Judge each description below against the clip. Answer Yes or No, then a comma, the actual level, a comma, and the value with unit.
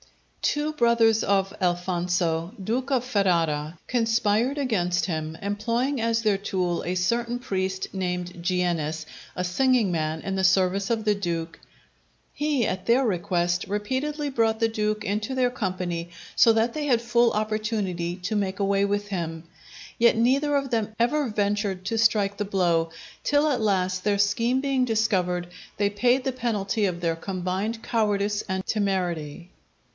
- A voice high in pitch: Yes, high, 205 Hz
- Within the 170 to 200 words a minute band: No, average, 155 wpm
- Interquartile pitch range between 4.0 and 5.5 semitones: Yes, average, 4.3 semitones